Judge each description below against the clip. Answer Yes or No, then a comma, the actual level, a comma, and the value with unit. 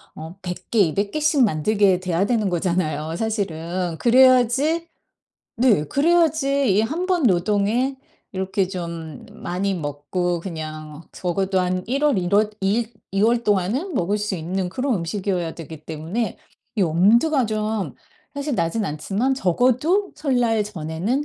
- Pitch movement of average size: No, wide, 5.9 semitones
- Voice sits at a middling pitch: No, high, 200 Hz